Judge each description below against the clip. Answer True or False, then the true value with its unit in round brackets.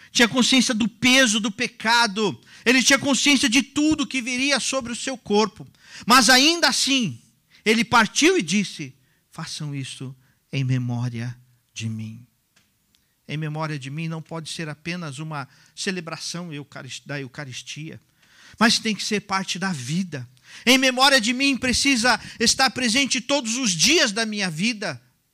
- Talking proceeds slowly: False (145 wpm)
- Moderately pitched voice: False (205 Hz)